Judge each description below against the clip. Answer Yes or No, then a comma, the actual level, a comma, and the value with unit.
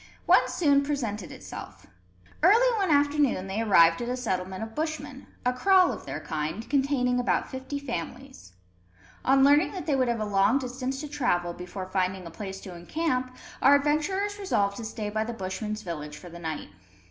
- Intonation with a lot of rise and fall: Yes, wide, 6.9 semitones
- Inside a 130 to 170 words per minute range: No, average, 180 wpm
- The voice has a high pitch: Yes, high, 245 Hz